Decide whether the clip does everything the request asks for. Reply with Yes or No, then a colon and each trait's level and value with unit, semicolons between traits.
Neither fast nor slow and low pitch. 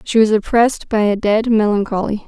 No: average, 185 wpm; high, 215 Hz